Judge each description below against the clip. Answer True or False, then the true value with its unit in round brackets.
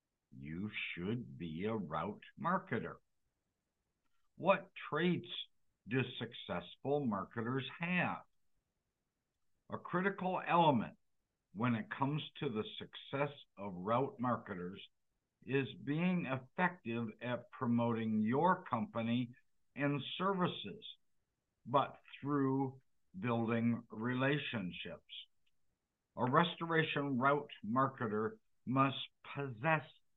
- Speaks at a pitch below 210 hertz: True (135 Hz)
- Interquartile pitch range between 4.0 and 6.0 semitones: True (5.0 semitones)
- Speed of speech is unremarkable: False (85 wpm)